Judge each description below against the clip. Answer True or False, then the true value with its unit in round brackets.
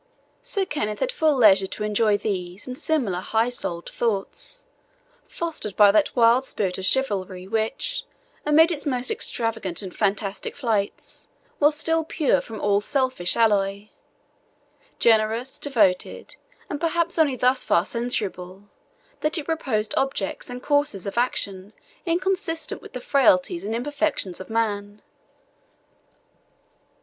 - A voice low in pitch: False (230 Hz)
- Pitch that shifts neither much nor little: False (6.3 semitones)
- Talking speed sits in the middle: False (130 wpm)